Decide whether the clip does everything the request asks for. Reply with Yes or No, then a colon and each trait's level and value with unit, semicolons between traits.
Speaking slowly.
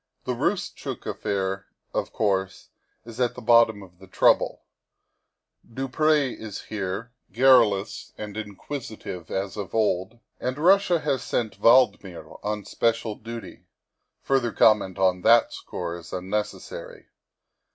Yes: slow, 125 wpm